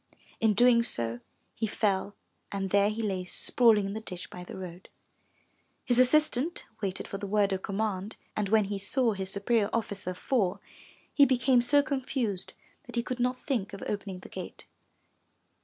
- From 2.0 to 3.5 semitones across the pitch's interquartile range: No, average, 3.9 semitones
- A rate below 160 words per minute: No, average, 175 wpm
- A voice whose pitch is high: Yes, high, 210 Hz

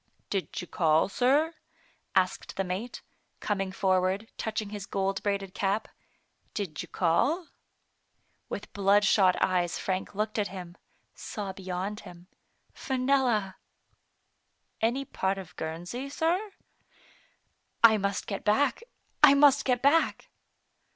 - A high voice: Yes, high, 200 Hz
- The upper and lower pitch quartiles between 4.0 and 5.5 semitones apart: Yes, average, 4.8 semitones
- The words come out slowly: Yes, slow, 125 wpm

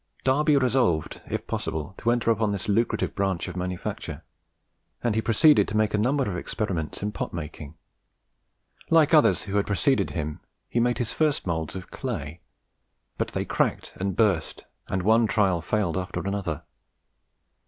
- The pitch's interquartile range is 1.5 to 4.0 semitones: No, average, 5.0 semitones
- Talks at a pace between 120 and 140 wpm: No, average, 165 wpm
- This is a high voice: No, low, 105 Hz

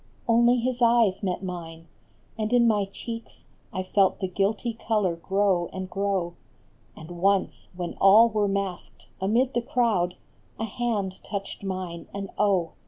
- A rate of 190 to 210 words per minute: No, average, 150 wpm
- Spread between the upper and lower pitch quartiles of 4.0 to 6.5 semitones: No, average, 3.5 semitones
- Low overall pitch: No, high, 200 Hz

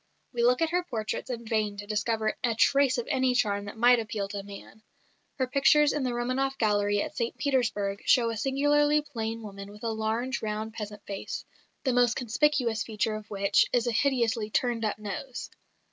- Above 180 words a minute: Yes, average, 190 wpm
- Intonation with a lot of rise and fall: No, average, 3.2 semitones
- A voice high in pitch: Yes, high, 230 Hz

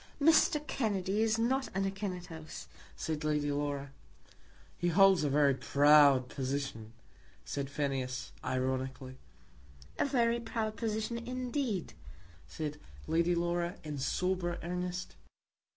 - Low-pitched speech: No, medium, 170 Hz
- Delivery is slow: Yes, slow, 110 wpm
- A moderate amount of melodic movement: No, wide, 7.1 semitones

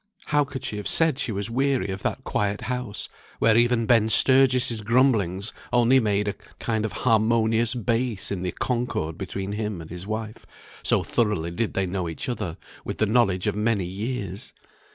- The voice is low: Yes, low, 110 Hz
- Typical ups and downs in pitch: Yes, average, 3.7 semitones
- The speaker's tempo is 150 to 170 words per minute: No, average, 180 wpm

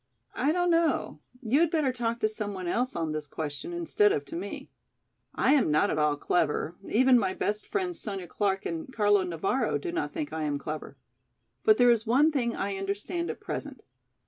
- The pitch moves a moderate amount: No, wide, 8.6 semitones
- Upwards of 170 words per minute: Yes, average, 200 wpm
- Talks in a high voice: Yes, high, 225 Hz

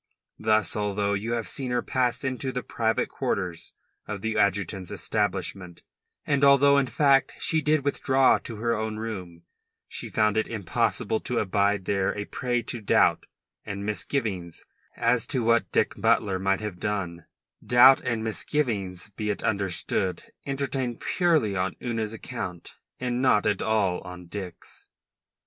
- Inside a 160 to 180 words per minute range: No, average, 150 wpm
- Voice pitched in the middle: No, low, 110 Hz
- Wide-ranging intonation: No, average, 4.0 semitones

